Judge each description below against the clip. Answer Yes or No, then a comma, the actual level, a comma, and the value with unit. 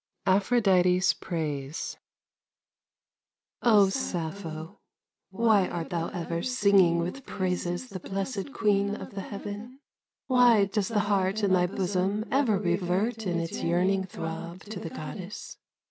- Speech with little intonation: No, average, 3.0 semitones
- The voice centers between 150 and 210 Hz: Yes, high, 190 Hz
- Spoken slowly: Yes, slow, 125 wpm